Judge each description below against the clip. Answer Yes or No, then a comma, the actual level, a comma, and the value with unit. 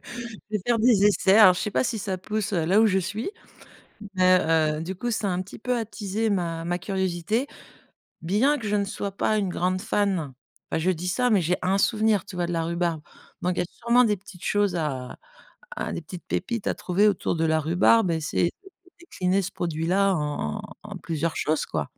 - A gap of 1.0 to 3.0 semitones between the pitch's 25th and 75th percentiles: No, average, 3.6 semitones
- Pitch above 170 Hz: Yes, high, 190 Hz